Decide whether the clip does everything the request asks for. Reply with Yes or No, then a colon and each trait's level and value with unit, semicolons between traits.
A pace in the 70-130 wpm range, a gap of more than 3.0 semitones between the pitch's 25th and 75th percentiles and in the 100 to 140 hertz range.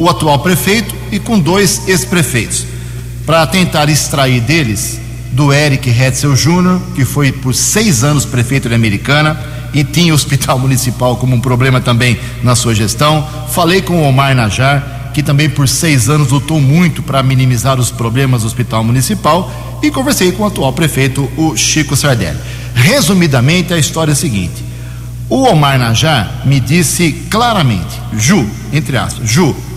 No: average, 160 wpm; average, 4.2 semitones; low, 135 Hz